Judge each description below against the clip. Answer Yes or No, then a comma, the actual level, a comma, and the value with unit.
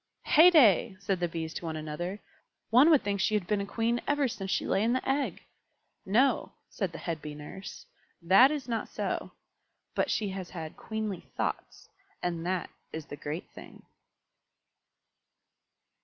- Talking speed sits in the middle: Yes, average, 165 wpm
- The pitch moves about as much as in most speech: No, wide, 5.7 semitones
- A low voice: No, high, 195 Hz